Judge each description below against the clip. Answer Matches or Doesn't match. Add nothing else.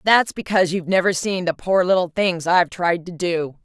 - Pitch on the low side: Doesn't match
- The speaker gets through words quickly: Matches